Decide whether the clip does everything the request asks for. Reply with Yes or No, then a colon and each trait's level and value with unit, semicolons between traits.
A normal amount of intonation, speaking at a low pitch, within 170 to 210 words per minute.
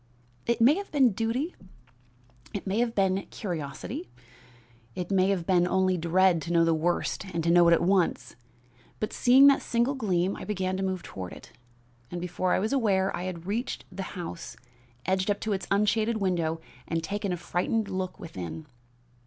No: average, 3.4 semitones; high, 190 Hz; average, 180 wpm